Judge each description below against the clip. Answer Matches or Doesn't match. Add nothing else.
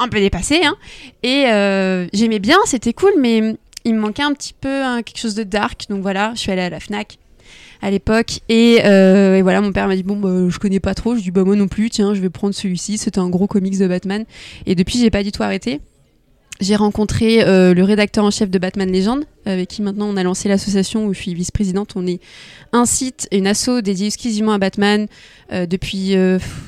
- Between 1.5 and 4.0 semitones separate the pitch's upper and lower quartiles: Matches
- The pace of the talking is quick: Matches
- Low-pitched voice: Doesn't match